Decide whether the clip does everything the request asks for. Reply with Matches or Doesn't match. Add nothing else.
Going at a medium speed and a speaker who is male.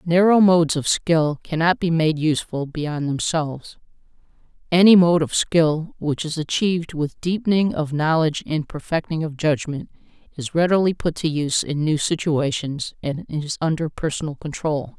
Doesn't match